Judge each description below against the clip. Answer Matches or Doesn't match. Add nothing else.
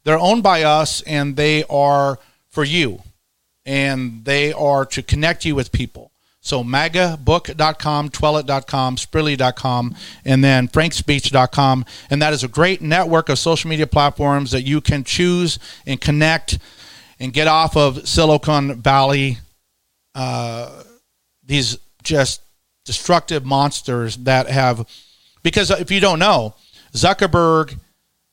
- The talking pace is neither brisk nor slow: Doesn't match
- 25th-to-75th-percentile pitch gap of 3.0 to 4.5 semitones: Matches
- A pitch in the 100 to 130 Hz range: Doesn't match